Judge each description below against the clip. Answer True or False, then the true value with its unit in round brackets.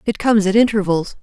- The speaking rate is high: False (195 wpm)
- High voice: True (205 Hz)